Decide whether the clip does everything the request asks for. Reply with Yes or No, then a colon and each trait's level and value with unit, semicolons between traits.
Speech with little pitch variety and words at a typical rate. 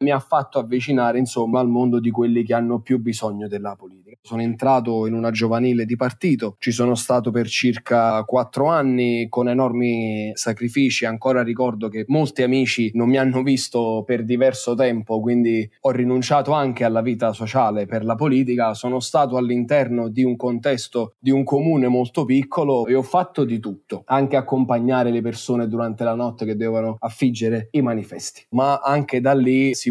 No: narrow, 2.2 semitones; fast, 175 wpm